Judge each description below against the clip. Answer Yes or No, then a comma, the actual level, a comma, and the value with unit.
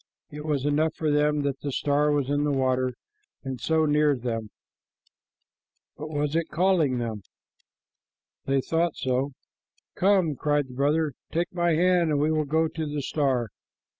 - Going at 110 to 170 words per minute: Yes, average, 165 wpm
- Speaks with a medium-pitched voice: Yes, medium, 150 Hz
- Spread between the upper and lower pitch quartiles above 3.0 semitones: No, average, 2.7 semitones